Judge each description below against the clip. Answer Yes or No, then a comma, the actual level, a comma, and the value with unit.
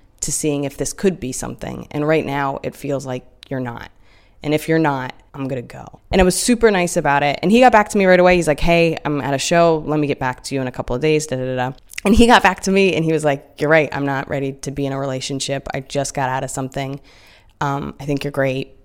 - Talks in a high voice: No, medium, 140 Hz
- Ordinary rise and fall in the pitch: Yes, average, 3.2 semitones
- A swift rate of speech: Yes, fast, 285 wpm